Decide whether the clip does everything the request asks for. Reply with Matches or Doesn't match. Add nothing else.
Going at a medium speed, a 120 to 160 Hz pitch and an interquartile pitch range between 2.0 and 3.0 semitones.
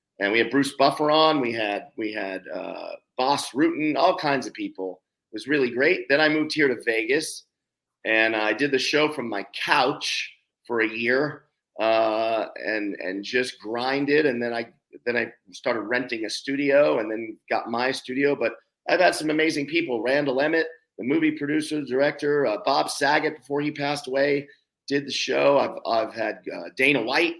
Doesn't match